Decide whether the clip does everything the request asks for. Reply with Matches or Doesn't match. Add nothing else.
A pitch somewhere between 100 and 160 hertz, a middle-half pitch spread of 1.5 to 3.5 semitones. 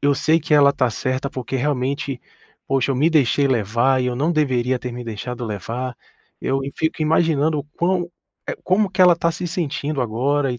Doesn't match